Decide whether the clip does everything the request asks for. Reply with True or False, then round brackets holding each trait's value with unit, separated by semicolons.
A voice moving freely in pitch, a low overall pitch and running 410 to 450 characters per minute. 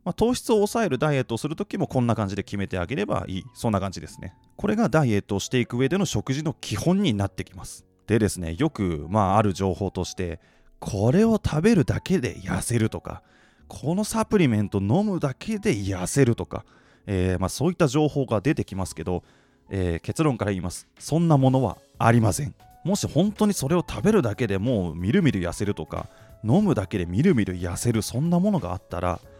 True (8.7 semitones; 115 Hz; 415 characters per minute)